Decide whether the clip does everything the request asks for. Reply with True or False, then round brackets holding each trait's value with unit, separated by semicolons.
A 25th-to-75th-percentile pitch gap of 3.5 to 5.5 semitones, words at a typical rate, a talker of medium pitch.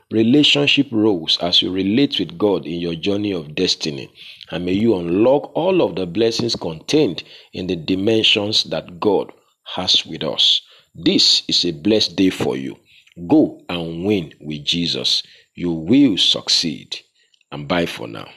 False (4.6 semitones; 155 wpm; 100 Hz)